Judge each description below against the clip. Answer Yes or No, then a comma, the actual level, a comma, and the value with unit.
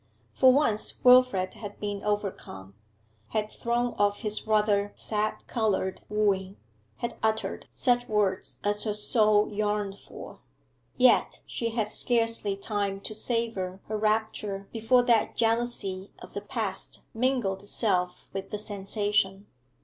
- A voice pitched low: No, high, 210 Hz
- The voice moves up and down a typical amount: No, narrow, 2.3 semitones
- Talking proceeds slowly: Yes, slow, 130 wpm